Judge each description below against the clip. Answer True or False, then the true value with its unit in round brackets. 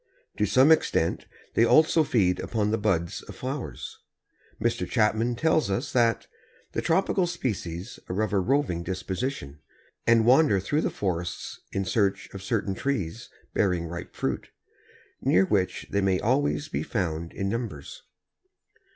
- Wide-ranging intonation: True (5.8 semitones)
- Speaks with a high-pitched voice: False (105 Hz)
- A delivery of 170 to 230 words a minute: False (145 wpm)